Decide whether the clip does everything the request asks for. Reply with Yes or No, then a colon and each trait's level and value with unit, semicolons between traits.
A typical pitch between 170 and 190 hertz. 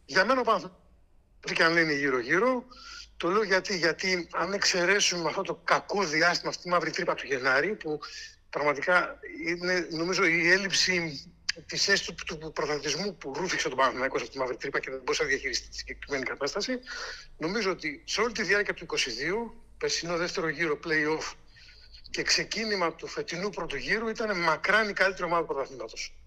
Yes: medium, 185 Hz